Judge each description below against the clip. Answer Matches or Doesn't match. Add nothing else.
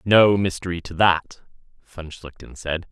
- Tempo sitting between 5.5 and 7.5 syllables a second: Doesn't match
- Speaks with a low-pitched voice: Matches